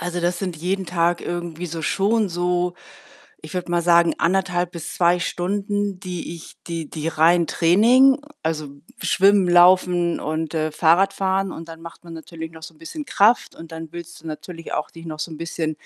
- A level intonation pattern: Yes, narrow, 2.0 semitones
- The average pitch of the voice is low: No, medium, 175 Hz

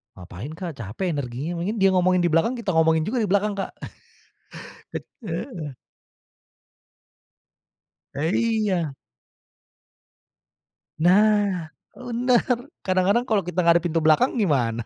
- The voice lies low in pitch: No, medium, 180 Hz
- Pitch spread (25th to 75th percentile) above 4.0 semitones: Yes, average, 5.0 semitones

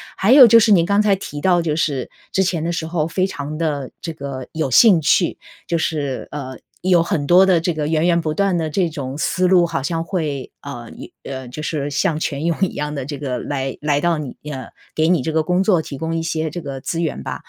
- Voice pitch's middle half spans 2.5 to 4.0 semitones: Yes, average, 3.4 semitones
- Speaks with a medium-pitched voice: Yes, medium, 160 Hz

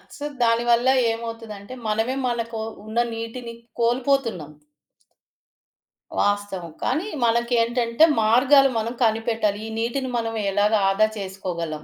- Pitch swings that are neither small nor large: No, narrow, 2.2 semitones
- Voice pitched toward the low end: No, high, 230 Hz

